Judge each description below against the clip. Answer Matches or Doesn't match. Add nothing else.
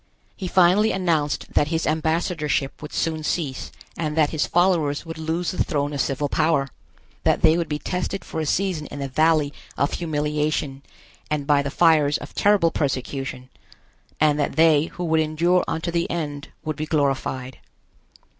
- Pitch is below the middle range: Doesn't match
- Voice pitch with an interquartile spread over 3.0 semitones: Doesn't match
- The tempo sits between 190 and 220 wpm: Doesn't match